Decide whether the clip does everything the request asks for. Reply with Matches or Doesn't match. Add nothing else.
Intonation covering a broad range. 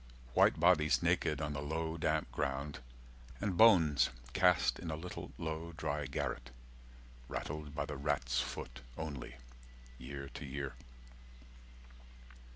Doesn't match